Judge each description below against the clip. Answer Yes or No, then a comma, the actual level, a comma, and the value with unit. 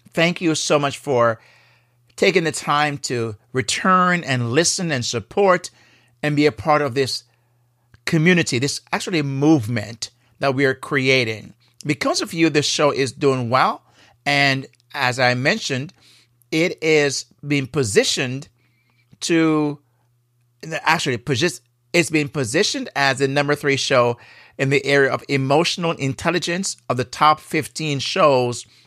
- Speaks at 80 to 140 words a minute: Yes, slow, 135 wpm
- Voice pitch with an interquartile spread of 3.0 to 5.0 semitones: Yes, average, 4.1 semitones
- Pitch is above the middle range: No, medium, 140 Hz